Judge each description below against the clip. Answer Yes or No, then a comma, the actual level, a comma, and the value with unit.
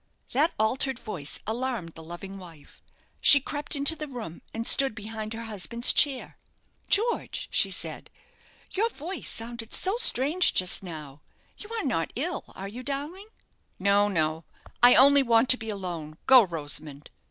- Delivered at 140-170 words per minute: Yes, average, 155 wpm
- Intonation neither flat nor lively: No, wide, 7.3 semitones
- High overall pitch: Yes, high, 230 Hz